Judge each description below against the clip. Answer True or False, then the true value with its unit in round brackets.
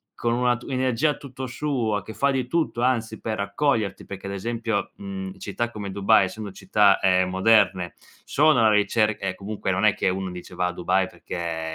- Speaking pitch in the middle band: False (105 Hz)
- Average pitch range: True (3.8 semitones)